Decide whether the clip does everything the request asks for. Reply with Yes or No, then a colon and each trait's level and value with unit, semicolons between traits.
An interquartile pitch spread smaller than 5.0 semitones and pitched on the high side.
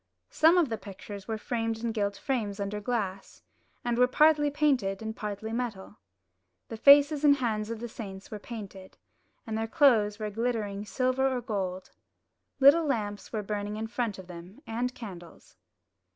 Yes: average, 3.6 semitones; high, 220 Hz